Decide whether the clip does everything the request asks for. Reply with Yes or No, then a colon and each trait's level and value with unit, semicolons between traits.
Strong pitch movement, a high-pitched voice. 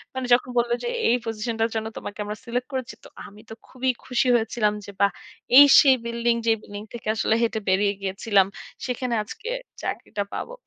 No: average, 3.0 semitones; high, 230 Hz